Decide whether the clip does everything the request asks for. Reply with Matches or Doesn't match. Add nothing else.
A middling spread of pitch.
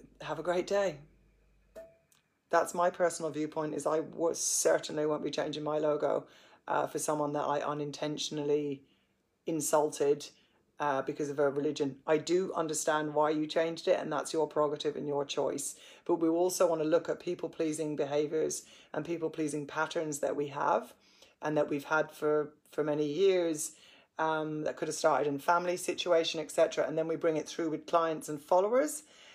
Doesn't match